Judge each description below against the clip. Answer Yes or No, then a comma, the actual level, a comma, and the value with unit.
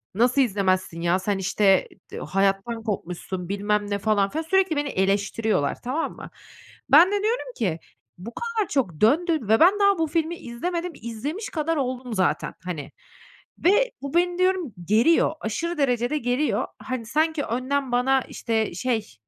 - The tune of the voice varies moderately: No, wide, 8.1 semitones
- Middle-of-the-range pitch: No, high, 245 Hz